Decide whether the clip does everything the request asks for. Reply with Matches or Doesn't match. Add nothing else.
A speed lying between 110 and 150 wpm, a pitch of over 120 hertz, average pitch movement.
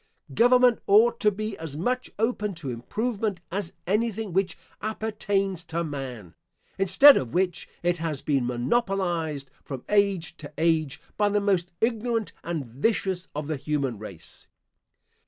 Doesn't match